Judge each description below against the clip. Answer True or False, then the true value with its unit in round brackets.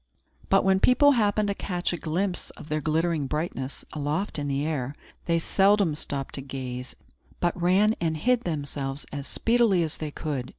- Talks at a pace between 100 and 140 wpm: False (175 wpm)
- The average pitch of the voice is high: False (160 Hz)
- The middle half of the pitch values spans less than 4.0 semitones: False (5.1 semitones)